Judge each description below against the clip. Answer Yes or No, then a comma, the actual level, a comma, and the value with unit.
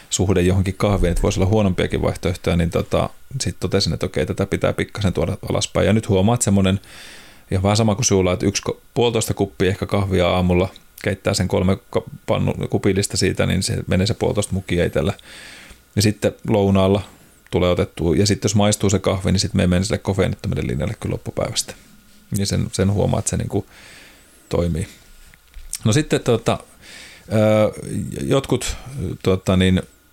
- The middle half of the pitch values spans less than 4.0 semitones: Yes, narrow, 2.4 semitones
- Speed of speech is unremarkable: No, fast, 165 wpm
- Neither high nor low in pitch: No, low, 100 Hz